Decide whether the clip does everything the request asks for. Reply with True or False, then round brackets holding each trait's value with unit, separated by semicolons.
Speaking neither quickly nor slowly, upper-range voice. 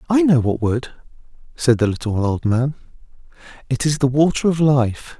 False (175 wpm; 135 Hz)